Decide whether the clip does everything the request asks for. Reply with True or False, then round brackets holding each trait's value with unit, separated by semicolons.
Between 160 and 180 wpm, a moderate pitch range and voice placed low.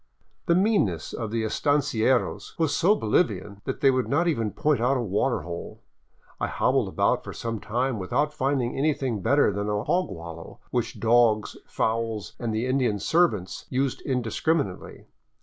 True (165 wpm; 5.0 semitones; 120 Hz)